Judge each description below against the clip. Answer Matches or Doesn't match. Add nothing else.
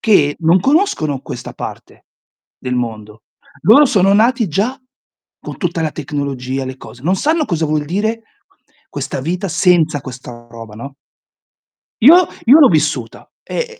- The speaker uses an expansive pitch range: Matches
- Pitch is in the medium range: Matches